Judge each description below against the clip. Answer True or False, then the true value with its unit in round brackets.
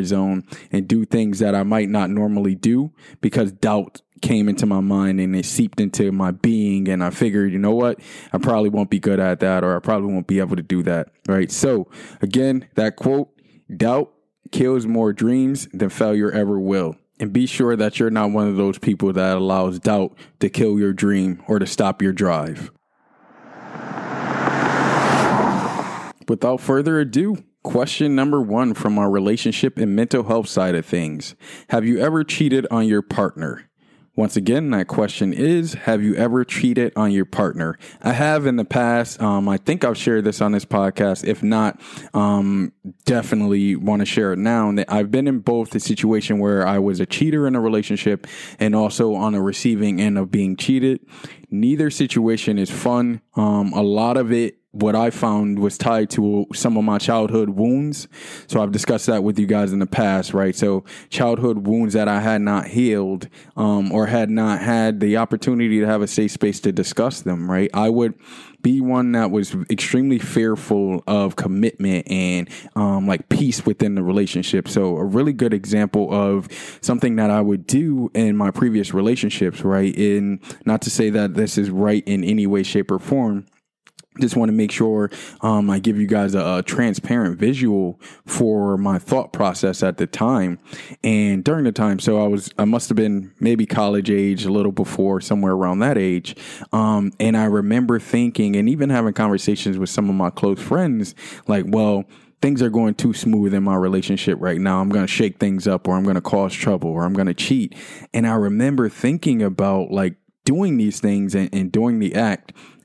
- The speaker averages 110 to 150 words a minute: False (190 wpm)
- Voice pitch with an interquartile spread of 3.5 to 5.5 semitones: False (2.7 semitones)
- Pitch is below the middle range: True (105 Hz)